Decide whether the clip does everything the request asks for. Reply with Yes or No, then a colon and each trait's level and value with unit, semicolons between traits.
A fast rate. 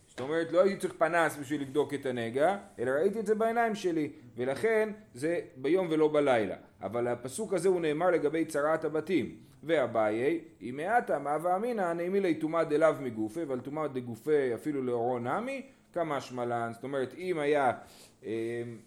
Yes: fast, 160 wpm